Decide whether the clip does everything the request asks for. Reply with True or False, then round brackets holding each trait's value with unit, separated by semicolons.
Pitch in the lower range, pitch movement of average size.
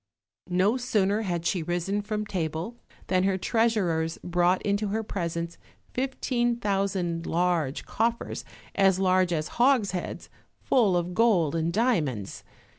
False (190 Hz; 4.2 semitones)